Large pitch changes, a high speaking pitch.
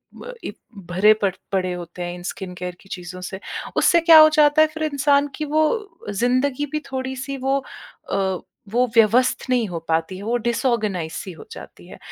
Yes: wide, 7.6 semitones; high, 240 Hz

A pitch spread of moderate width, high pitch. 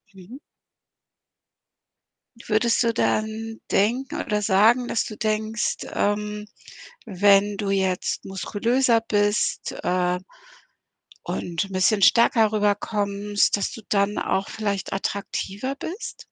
No: narrow, 2.1 semitones; high, 210 Hz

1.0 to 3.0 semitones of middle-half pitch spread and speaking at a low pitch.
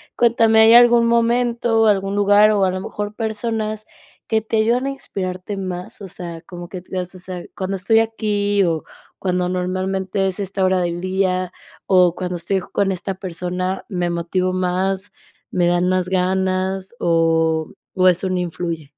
No: narrow, 2.5 semitones; medium, 185 Hz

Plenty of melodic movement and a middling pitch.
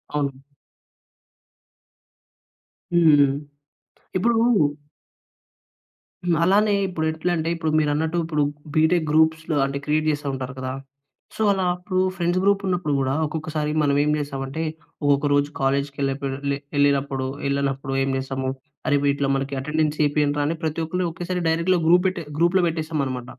No: average, 3.3 semitones; medium, 150 Hz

